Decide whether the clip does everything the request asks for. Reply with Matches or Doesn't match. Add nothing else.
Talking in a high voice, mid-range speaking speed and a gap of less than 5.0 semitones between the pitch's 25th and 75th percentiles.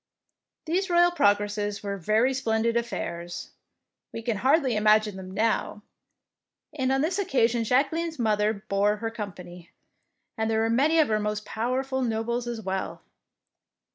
Matches